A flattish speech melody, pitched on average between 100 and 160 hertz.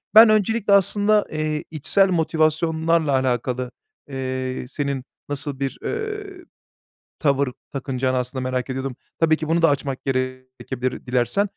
No: average, 4.4 semitones; medium, 140 Hz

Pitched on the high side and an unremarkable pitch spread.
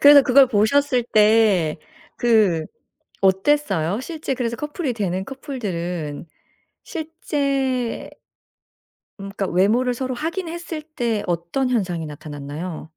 No: high, 230 Hz; wide, 7.4 semitones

